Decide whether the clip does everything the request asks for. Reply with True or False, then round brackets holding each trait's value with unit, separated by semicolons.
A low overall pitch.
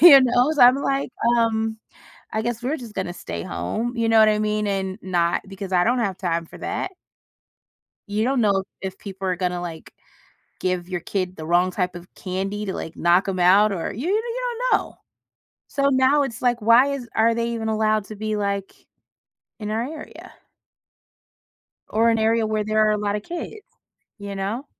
False (215 Hz)